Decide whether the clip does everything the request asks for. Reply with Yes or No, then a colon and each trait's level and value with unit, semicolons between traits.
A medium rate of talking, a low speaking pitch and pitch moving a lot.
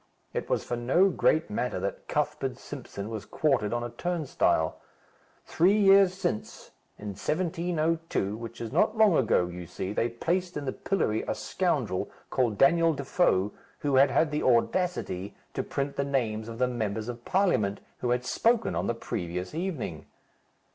Yes: average, 165 wpm; low, 130 Hz; wide, 7.8 semitones